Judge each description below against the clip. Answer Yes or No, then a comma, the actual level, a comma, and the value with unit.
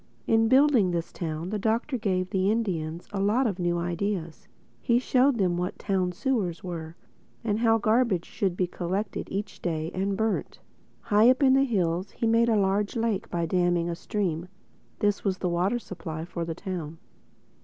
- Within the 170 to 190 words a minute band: Yes, average, 180 wpm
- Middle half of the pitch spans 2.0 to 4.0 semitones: No, average, 4.4 semitones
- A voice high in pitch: Yes, high, 195 Hz